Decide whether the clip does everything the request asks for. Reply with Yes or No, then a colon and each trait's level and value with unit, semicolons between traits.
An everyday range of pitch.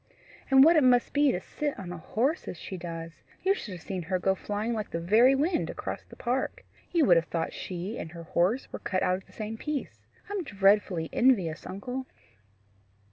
No: wide, 6.9 semitones